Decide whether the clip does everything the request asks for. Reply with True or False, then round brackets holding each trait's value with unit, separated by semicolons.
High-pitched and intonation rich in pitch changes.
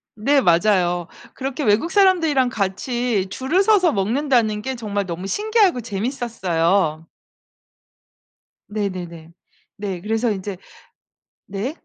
True (215 Hz; 5.8 semitones)